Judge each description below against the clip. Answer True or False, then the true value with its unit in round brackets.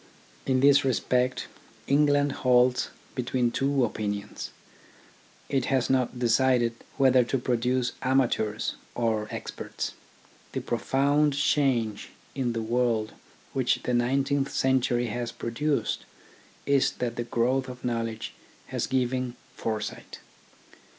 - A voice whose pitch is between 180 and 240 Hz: False (125 Hz)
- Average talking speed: False (110 wpm)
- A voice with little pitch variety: True (2.2 semitones)